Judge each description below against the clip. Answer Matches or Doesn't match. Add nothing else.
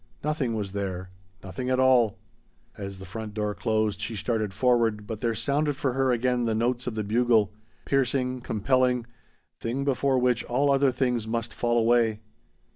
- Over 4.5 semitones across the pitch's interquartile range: Doesn't match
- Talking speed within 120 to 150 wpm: Doesn't match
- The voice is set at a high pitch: Doesn't match